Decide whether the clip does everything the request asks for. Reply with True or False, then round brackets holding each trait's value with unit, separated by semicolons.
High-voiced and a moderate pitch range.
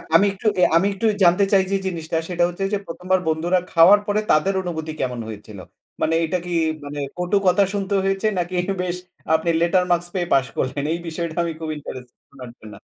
False (175 Hz; 3.0 semitones)